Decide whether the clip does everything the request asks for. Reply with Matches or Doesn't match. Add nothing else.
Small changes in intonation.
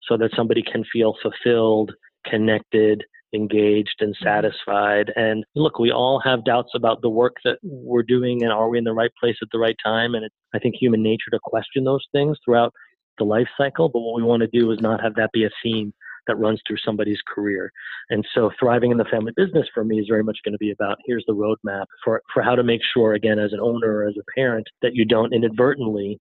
Matches